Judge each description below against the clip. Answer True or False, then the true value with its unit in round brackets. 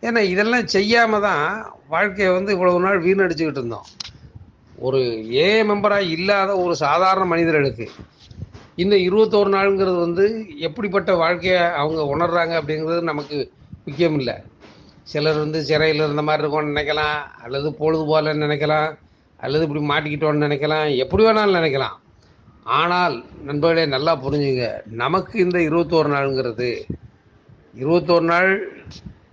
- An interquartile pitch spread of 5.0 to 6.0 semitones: False (4.0 semitones)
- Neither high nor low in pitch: True (165 Hz)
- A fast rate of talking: False (115 wpm)